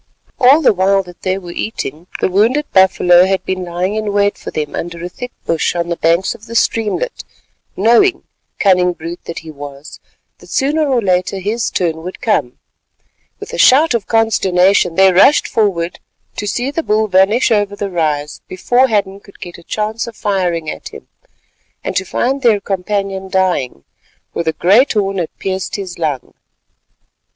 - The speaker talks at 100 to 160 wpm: No, average, 175 wpm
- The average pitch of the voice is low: No, high, 190 Hz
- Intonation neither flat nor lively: Yes, average, 3.9 semitones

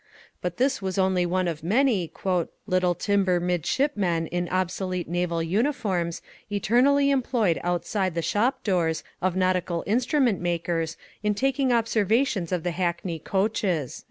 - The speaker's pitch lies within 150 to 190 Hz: Yes, medium, 185 Hz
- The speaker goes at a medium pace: No, slow, 130 wpm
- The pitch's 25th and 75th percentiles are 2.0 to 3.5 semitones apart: No, average, 4.0 semitones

